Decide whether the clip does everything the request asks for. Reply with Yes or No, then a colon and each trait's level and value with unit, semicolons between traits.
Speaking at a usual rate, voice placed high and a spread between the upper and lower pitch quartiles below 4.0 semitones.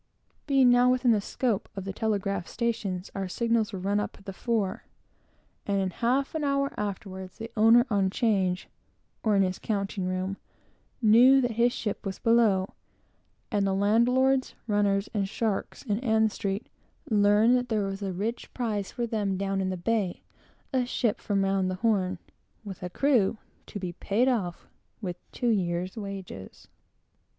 Yes: average, 170 wpm; high, 205 Hz; average, 3.3 semitones